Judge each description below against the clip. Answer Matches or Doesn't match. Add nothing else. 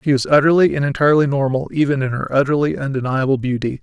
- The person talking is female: Doesn't match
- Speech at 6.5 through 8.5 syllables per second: Matches